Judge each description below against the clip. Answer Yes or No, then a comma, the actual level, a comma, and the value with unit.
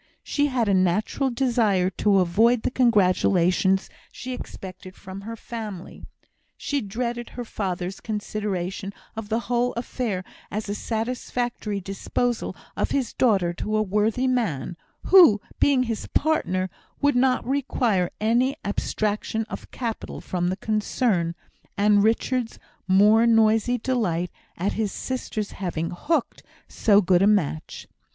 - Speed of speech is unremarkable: No, slow, 130 wpm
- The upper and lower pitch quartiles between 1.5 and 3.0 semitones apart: No, average, 4.1 semitones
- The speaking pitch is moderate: No, high, 215 Hz